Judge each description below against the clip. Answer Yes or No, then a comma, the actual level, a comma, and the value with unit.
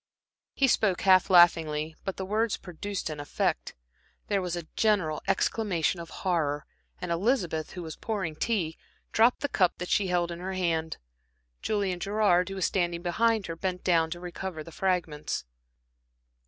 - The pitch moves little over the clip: No, average, 3.0 semitones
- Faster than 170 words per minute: No, average, 165 wpm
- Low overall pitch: No, medium, 180 Hz